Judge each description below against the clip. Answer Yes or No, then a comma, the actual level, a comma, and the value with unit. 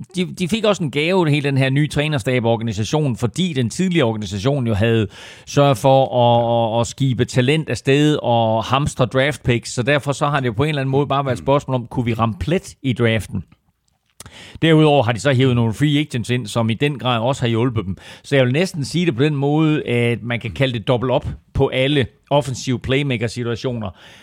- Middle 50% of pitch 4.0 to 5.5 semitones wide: No, average, 3.5 semitones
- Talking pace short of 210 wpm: No, average, 215 wpm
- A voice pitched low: Yes, low, 130 Hz